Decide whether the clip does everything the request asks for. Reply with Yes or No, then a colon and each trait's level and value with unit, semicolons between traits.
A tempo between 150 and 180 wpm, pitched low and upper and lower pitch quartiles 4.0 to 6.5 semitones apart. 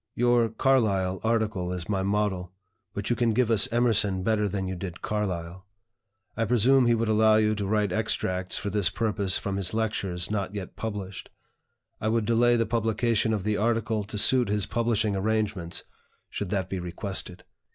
No: average, 175 wpm; low, 105 Hz; average, 2.9 semitones